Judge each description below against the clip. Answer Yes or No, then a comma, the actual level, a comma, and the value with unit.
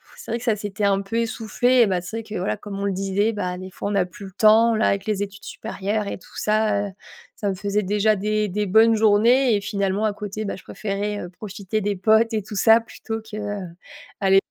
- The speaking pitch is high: Yes, high, 210 Hz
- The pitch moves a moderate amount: No, narrow, 1.8 semitones